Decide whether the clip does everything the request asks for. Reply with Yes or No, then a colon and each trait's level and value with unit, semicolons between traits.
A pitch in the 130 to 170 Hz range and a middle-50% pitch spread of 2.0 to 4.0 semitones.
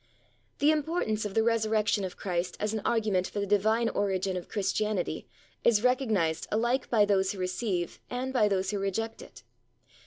No: high, 210 Hz; average, 2.9 semitones